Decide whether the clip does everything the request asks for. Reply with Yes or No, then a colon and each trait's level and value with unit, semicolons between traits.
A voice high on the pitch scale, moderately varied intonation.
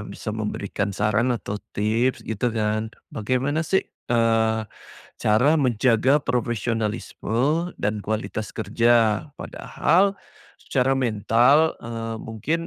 No: low, 115 Hz; average, 3.0 semitones